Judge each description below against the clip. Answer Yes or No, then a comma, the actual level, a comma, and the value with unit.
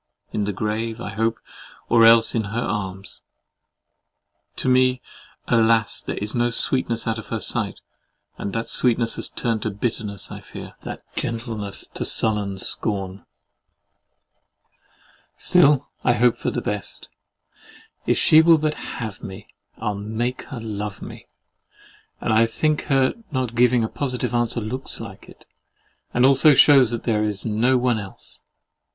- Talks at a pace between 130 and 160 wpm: Yes, average, 150 wpm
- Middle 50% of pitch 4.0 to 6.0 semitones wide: No, average, 2.9 semitones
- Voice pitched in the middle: No, low, 115 Hz